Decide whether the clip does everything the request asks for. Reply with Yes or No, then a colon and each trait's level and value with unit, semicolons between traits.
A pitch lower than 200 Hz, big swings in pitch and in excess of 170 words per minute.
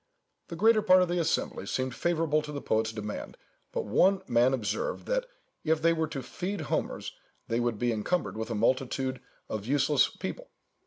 Yes: medium, 140 Hz; wide, 6.6 semitones; average, 180 wpm